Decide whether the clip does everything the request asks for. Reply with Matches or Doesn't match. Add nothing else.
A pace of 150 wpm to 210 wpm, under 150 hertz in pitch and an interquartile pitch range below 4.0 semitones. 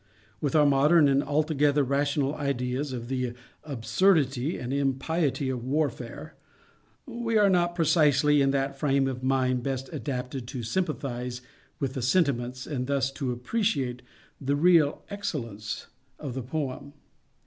Doesn't match